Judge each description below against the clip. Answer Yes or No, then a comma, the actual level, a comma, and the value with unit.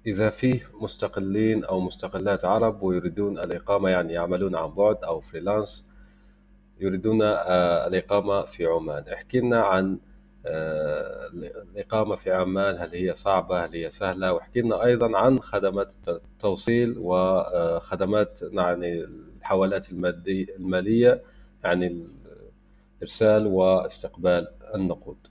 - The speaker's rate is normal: Yes, average, 100 wpm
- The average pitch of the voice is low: Yes, very low, 95 Hz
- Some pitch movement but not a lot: Yes, average, 3.2 semitones